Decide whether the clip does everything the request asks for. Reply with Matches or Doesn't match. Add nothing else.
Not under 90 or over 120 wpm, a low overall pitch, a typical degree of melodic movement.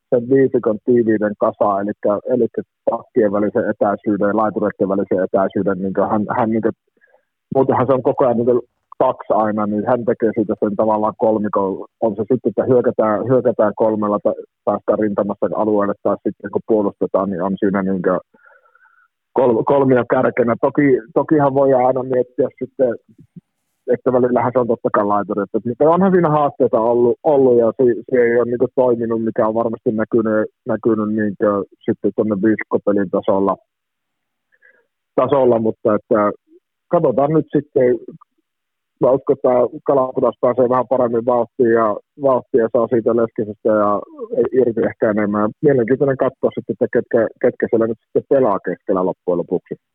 Doesn't match